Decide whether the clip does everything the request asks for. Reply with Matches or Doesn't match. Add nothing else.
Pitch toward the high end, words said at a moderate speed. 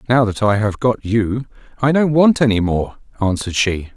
Doesn't match